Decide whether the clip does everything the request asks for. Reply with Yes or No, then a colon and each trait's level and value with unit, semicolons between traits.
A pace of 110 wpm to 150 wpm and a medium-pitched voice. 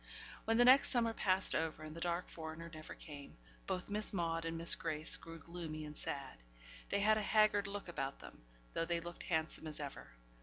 No: average, 200 wpm; medium, 170 Hz